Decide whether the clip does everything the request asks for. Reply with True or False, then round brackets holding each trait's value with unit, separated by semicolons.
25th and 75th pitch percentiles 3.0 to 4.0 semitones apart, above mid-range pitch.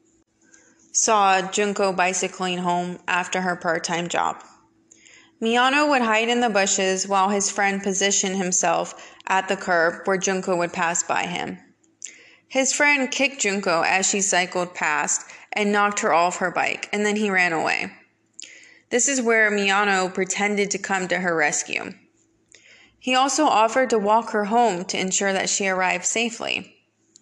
True (3.7 semitones; 195 Hz)